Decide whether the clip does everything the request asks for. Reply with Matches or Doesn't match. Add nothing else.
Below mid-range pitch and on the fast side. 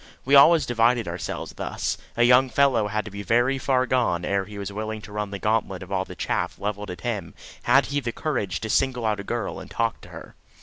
Matches